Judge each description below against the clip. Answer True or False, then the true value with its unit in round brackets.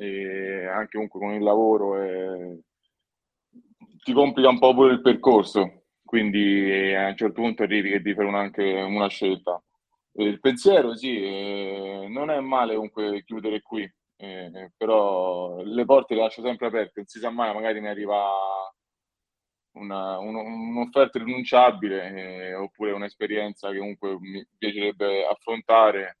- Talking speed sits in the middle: True (150 wpm)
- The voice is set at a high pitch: False (105 Hz)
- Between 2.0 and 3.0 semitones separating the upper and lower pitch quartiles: True (2.7 semitones)